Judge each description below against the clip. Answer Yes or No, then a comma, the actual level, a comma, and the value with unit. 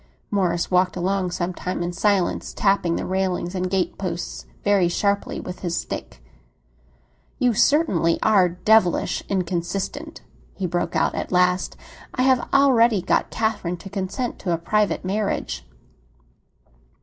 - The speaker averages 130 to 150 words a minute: Yes, slow, 135 wpm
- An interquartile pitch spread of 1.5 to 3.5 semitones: Yes, average, 2.9 semitones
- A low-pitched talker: No, medium, 185 Hz